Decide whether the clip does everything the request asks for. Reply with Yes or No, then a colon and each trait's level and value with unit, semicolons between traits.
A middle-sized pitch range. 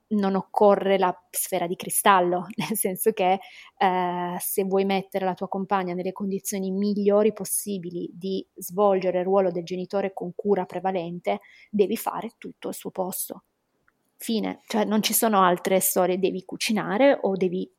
No: narrow, 1.9 semitones